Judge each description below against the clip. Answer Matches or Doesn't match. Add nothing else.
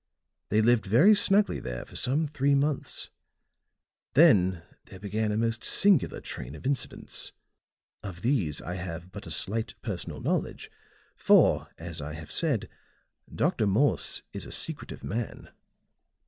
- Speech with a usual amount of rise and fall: Doesn't match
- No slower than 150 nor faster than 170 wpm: Doesn't match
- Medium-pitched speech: Doesn't match